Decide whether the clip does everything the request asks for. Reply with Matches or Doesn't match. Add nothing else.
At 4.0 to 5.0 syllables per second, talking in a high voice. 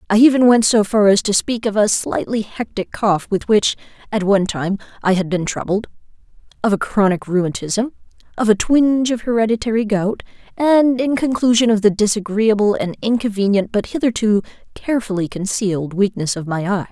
Doesn't match